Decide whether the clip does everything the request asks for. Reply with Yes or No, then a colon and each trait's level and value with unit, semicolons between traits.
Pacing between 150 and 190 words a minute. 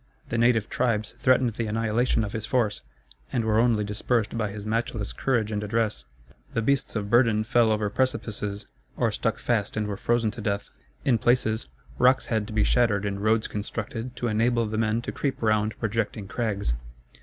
Yes: average, 185 wpm